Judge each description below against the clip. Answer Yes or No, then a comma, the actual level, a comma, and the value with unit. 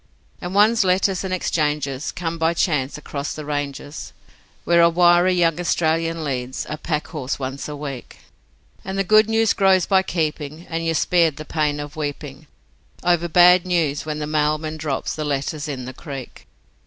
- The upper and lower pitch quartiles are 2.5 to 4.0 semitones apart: Yes, average, 3.2 semitones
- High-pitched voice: No, medium, 155 Hz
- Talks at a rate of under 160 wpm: No, average, 175 wpm